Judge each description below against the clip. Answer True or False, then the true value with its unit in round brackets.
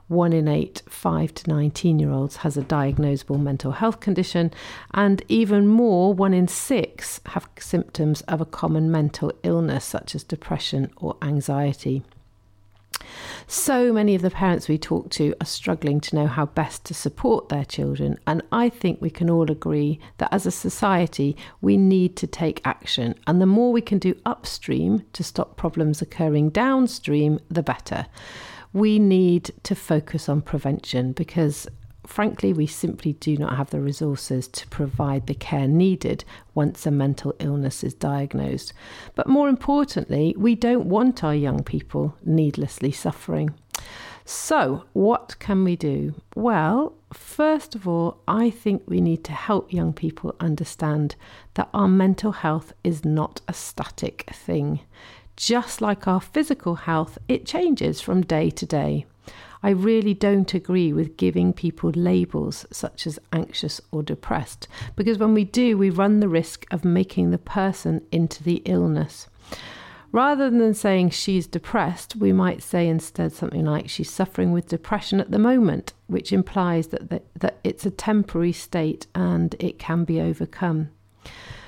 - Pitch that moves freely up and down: True (5.7 semitones)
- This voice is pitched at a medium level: True (160 Hz)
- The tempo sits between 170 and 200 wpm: False (160 wpm)